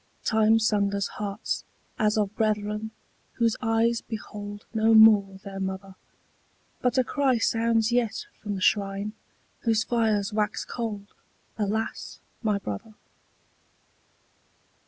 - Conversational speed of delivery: No, slow, 115 wpm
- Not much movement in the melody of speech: Yes, narrow, 1.8 semitones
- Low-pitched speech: No, high, 215 Hz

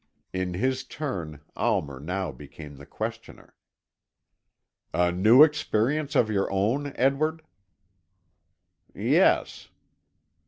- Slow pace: Yes, slow, 90 wpm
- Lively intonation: Yes, wide, 7.7 semitones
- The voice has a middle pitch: No, low, 105 Hz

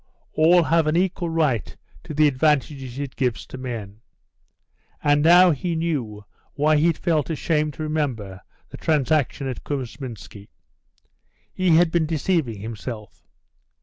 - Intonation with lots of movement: No, average, 4.6 semitones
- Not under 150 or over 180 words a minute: No, average, 140 wpm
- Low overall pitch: No, medium, 150 Hz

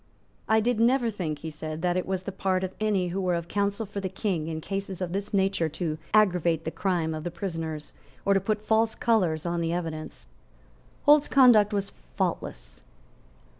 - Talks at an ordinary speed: Yes, average, 195 wpm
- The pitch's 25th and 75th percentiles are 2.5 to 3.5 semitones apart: No, average, 4.0 semitones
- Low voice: No, medium, 185 Hz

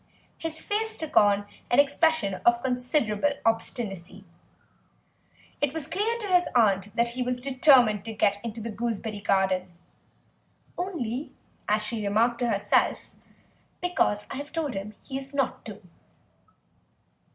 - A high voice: Yes, high, 235 Hz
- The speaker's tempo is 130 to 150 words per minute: Yes, average, 140 wpm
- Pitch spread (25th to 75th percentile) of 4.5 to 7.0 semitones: Yes, wide, 5.6 semitones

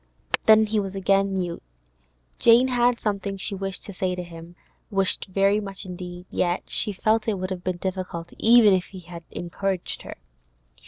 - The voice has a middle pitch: No, high, 195 Hz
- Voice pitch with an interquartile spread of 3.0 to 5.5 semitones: No, narrow, 2.5 semitones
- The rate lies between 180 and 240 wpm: No, average, 170 wpm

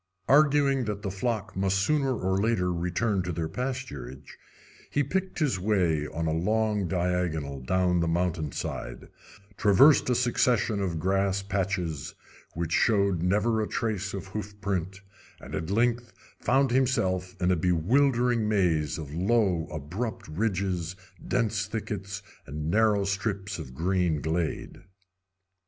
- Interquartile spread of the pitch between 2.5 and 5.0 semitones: Yes, average, 4.5 semitones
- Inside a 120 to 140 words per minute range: Yes, slow, 135 wpm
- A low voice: Yes, very low, 95 Hz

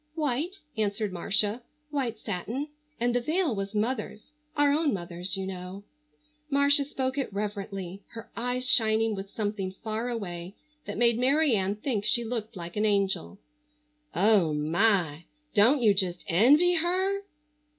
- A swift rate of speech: No, average, 140 wpm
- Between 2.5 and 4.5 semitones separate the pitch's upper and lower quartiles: No, average, 5.0 semitones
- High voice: Yes, high, 220 Hz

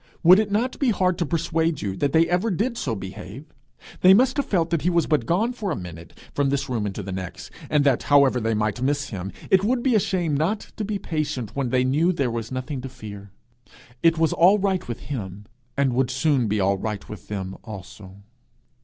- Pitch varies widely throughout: Yes, wide, 8.6 semitones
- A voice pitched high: No, medium, 140 Hz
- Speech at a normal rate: No, fast, 225 wpm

